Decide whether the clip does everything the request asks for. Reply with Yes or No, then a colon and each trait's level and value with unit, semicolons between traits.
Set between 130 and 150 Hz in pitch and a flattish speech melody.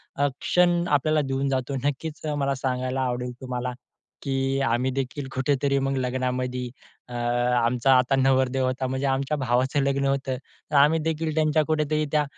Yes: low, 135 Hz; narrow, 2.2 semitones